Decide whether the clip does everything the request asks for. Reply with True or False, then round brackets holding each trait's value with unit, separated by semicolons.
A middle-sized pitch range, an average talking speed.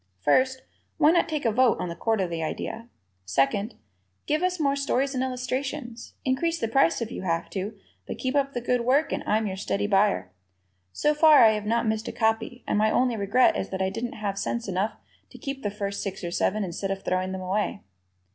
False (5.0 semitones; 215 wpm)